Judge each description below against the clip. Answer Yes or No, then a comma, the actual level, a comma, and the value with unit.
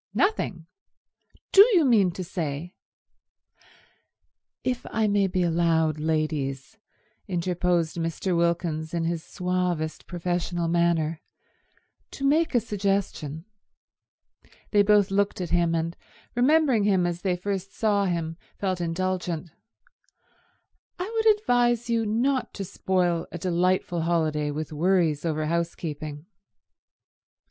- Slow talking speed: Yes, slow, 115 wpm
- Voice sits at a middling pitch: Yes, medium, 175 Hz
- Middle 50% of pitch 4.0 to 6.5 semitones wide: No, average, 3.5 semitones